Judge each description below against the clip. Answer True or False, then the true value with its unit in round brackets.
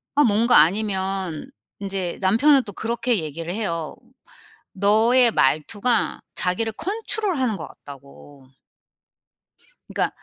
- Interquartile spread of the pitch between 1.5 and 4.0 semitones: False (5.6 semitones)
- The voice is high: True (205 Hz)